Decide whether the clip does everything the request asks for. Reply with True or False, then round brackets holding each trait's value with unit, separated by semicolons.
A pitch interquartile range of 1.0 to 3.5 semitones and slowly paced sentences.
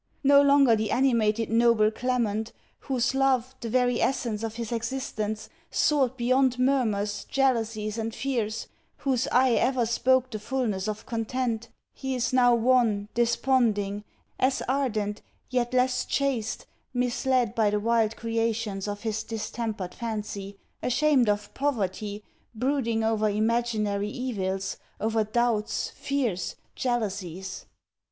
True (3.1 semitones; 125 wpm)